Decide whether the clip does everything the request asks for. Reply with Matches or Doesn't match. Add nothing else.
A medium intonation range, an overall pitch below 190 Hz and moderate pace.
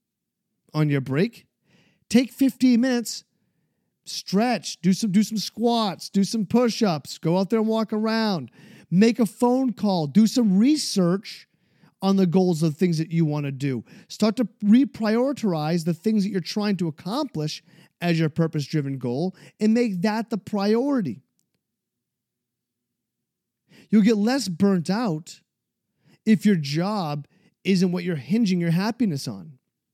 Doesn't match